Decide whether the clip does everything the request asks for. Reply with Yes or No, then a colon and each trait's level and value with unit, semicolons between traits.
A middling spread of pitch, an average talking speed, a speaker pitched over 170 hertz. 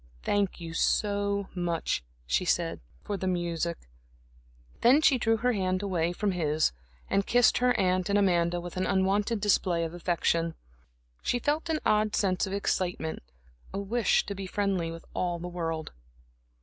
Yes: average, 3.0 semitones; average, 160 wpm; high, 190 Hz